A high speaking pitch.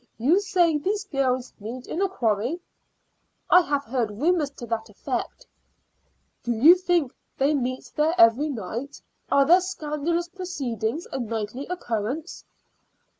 Yes: very high, 280 Hz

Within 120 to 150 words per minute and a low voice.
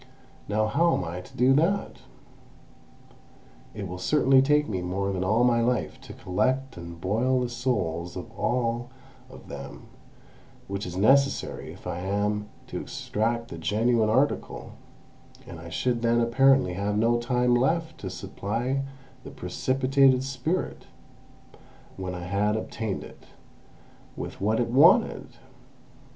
Yes: average, 140 wpm; low, 115 Hz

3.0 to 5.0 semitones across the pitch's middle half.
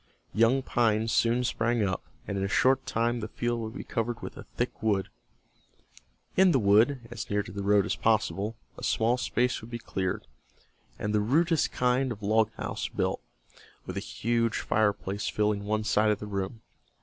No: narrow, 2.5 semitones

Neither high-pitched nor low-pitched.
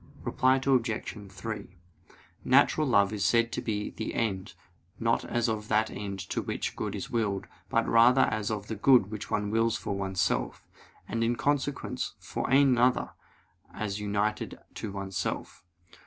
No: low, 110 Hz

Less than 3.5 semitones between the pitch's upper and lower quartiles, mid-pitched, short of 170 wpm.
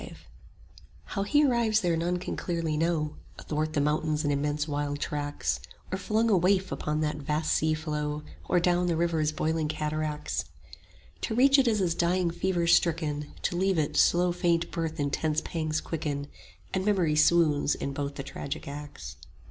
No: average, 2.8 semitones; medium, 160 Hz; average, 175 wpm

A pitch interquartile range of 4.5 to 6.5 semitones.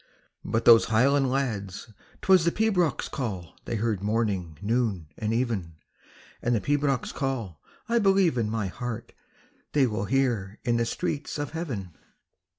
Yes: average, 5.0 semitones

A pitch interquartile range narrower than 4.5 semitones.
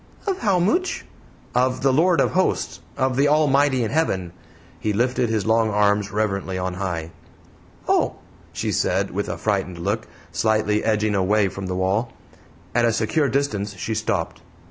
No: average, 5.2 semitones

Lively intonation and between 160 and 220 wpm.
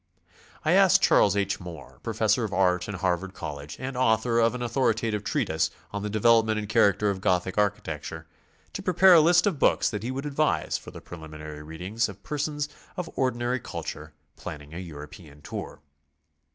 Yes: wide, 6.8 semitones; average, 180 wpm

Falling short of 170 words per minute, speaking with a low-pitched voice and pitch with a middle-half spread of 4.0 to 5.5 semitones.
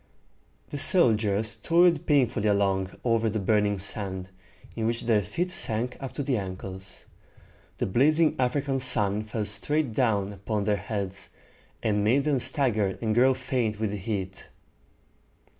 Yes: average, 145 wpm; low, 110 Hz; average, 4.3 semitones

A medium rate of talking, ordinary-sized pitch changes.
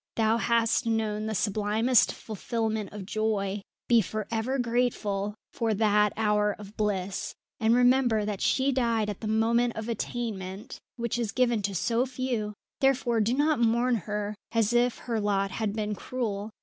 No: average, 160 wpm; narrow, 2.3 semitones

